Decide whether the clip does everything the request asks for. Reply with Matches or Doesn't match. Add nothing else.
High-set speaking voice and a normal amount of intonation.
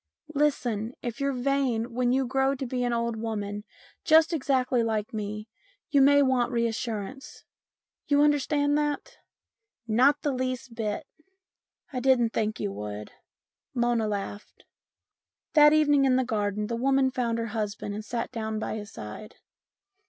Matches